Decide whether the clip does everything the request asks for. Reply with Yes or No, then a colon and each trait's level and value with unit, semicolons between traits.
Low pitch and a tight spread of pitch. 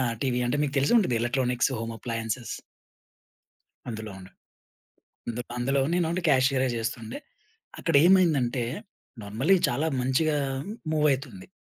No: low, 130 Hz; average, 3.9 semitones